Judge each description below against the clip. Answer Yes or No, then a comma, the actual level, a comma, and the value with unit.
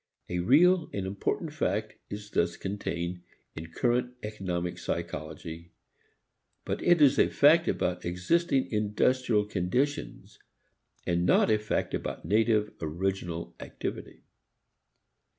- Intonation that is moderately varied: No, wide, 6.2 semitones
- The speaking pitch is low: Yes, low, 105 Hz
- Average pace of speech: No, slow, 115 wpm